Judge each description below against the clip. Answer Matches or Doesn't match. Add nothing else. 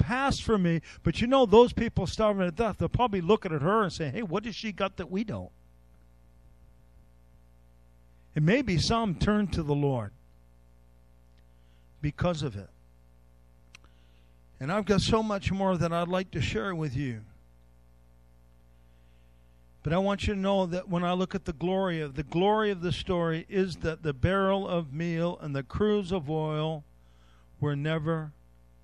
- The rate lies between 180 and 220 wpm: Doesn't match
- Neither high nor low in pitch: Matches